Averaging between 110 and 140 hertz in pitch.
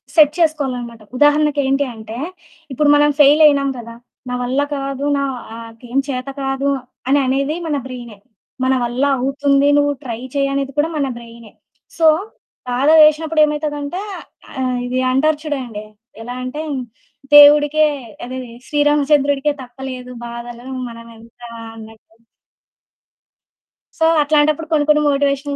No: very high, 275 Hz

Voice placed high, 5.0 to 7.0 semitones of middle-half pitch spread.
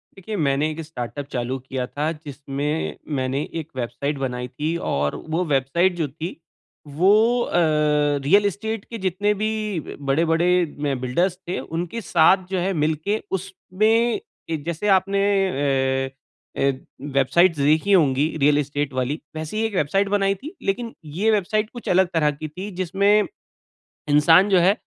No: medium, 165 Hz; average, 5.3 semitones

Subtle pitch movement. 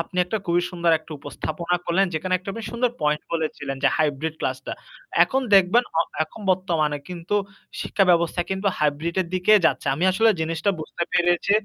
No: average, 3.2 semitones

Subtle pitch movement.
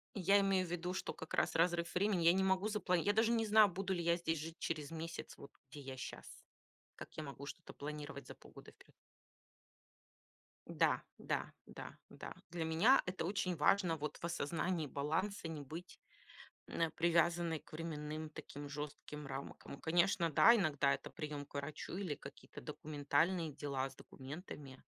No: average, 3.7 semitones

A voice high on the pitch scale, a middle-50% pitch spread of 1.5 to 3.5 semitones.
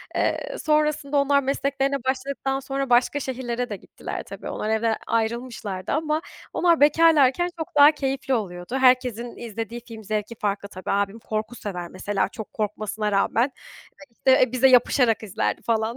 No: high, 245 Hz; average, 4.2 semitones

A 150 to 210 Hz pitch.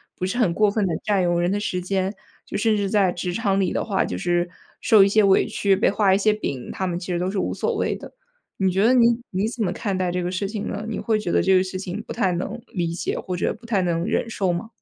Yes: high, 195 Hz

